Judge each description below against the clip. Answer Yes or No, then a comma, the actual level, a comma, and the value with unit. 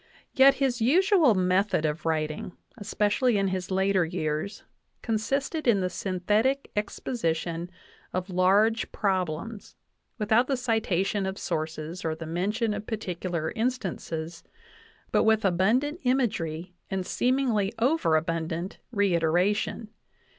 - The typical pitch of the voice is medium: No, high, 195 Hz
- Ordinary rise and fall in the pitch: Yes, average, 4.9 semitones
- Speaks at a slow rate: Yes, slow, 110 wpm